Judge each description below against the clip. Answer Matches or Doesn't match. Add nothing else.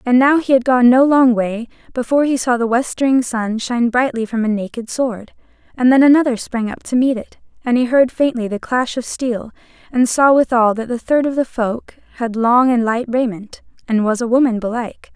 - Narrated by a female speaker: Matches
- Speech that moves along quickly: Matches